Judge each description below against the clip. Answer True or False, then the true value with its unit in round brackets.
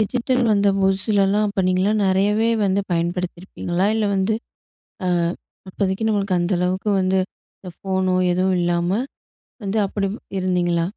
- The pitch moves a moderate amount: False (2.0 semitones)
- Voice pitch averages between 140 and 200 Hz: True (190 Hz)